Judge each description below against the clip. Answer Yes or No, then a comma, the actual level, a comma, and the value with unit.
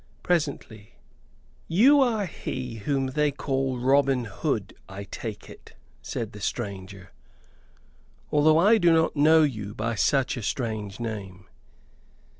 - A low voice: Yes, low, 130 Hz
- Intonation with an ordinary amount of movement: No, wide, 6.2 semitones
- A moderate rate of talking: No, slow, 125 wpm